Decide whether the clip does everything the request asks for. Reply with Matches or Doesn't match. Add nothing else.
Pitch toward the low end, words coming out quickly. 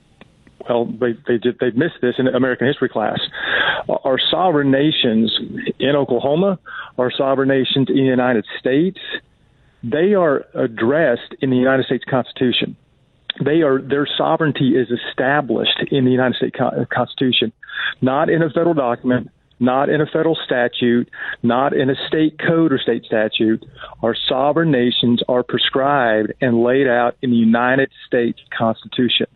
Doesn't match